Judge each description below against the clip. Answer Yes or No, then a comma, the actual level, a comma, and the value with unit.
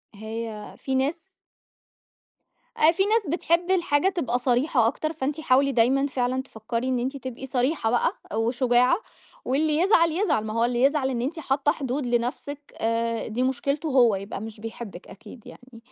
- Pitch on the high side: Yes, very high, 260 Hz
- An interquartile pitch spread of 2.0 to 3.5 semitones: No, average, 3.9 semitones